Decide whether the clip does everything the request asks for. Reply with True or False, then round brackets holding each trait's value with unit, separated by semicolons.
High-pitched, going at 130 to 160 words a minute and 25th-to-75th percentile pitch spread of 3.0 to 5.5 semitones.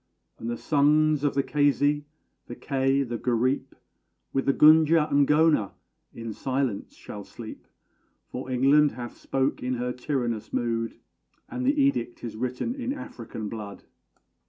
False (135 Hz; 145 wpm; 3.8 semitones)